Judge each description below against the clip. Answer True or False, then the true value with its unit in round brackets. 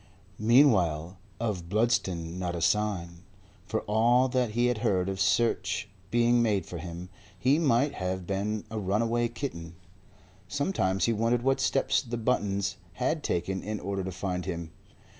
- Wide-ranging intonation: False (4.6 semitones)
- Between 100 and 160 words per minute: True (155 wpm)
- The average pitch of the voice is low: True (105 Hz)